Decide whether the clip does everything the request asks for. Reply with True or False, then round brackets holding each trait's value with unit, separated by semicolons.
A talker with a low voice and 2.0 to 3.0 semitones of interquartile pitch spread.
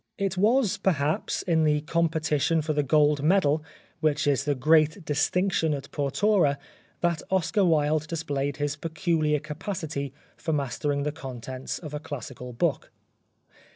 False (150 Hz; 2.5 semitones)